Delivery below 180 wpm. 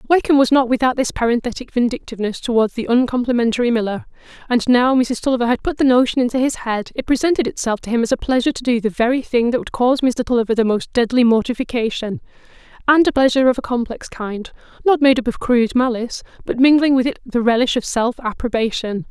No: fast, 205 wpm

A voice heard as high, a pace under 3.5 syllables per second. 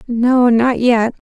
Yes: high, 240 Hz; 2.9 syllables/s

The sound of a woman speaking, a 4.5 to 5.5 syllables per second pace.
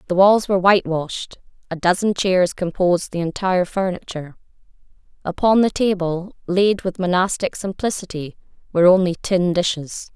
Yes: female; 5.4 syllables/s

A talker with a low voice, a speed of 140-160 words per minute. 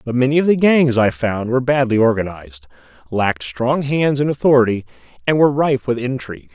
No: low, 125 Hz; average, 185 wpm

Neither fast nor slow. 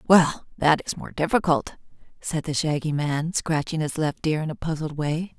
Yes: average, 190 wpm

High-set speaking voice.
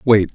No: low, 105 Hz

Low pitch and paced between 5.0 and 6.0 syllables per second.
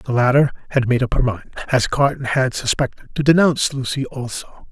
Yes: low, 130 Hz; 5.3 syllables/s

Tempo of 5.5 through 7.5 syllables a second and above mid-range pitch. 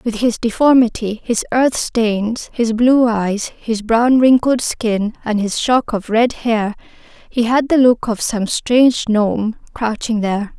No: 3.9 syllables/s; high, 230 Hz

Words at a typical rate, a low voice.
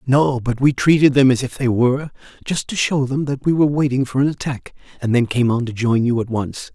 No: fast, 260 wpm; low, 130 Hz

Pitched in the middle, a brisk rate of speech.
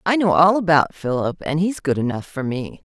Yes: medium, 160 Hz; fast, 230 wpm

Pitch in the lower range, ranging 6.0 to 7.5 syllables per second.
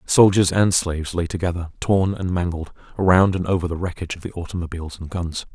Yes: very low, 90 Hz; 6.2 syllables/s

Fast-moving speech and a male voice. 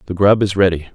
Yes: fast, 255 wpm; male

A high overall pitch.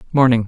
No: low, 125 Hz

